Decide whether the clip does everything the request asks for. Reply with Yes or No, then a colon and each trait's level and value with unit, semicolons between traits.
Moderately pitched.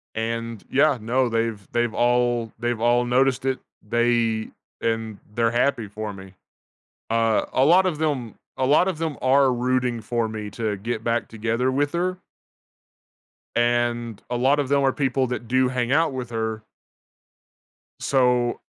No: low, 120 Hz